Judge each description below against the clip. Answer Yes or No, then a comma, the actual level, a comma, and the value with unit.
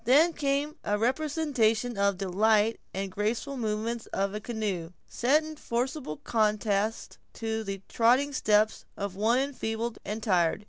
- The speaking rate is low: No, average, 145 wpm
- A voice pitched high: Yes, high, 220 Hz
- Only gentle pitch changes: No, average, 3.7 semitones